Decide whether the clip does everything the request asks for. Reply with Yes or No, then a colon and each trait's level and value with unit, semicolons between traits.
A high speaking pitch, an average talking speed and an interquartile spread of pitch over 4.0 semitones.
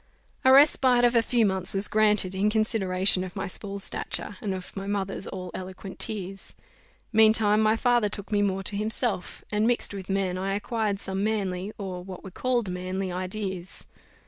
No: high, 200 Hz; average, 180 wpm; narrow, 2.4 semitones